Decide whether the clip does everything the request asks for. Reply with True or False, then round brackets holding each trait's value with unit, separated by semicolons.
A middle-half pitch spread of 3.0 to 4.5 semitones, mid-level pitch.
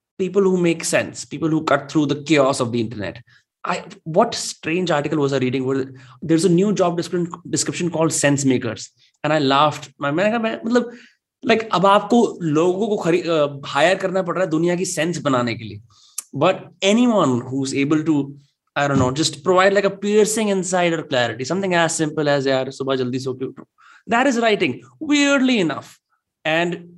False (5.4 semitones; 160 Hz)